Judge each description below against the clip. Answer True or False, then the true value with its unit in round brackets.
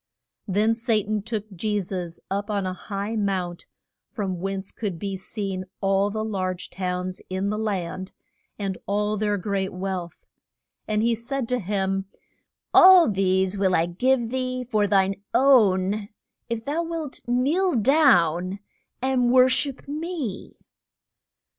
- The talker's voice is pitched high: True (205 Hz)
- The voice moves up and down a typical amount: True (4.0 semitones)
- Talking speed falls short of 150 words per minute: True (140 wpm)